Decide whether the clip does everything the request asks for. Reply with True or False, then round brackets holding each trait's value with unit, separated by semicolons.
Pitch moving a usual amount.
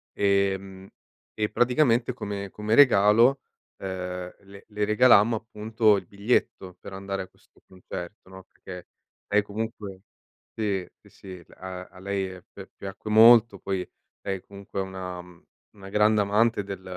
False (2.2 semitones)